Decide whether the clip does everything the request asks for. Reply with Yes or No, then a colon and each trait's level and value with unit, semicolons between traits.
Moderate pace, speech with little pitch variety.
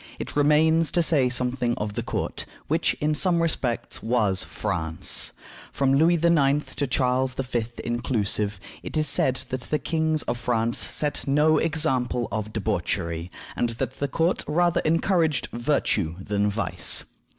No: average, 150 wpm; wide, 5.5 semitones